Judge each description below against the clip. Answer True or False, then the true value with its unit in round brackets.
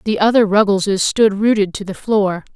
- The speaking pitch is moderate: False (205 Hz)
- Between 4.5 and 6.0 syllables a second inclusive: True (5.1 syllables/s)